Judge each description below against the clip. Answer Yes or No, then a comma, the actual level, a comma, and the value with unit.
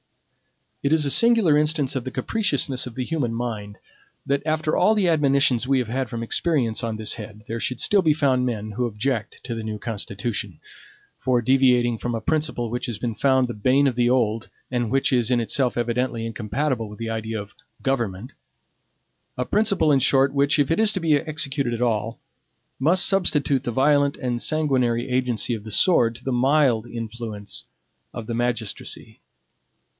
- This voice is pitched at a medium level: No, low, 125 Hz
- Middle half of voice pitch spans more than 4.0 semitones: No, average, 3.7 semitones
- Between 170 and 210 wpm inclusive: Yes, average, 185 wpm